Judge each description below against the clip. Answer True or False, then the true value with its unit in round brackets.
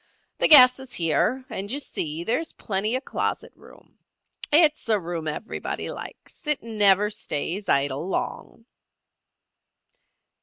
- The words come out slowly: True (130 wpm)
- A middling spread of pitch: False (7.0 semitones)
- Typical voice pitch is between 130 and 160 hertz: False (210 Hz)